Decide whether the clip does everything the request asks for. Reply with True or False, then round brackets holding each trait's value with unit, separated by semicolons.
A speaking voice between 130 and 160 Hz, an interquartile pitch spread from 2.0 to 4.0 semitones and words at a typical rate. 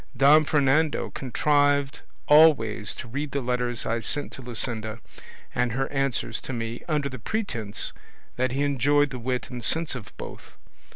True (135 Hz; 3.2 semitones; 160 wpm)